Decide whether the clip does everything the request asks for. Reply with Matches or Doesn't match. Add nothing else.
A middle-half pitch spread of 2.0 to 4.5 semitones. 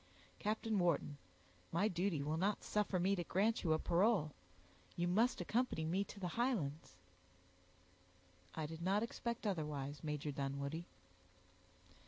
Doesn't match